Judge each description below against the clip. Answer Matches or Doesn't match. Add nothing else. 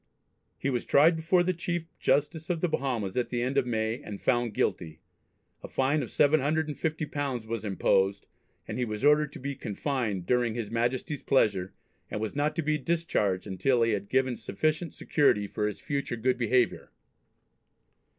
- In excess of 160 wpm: Matches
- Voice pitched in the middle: Doesn't match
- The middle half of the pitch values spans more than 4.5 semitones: Matches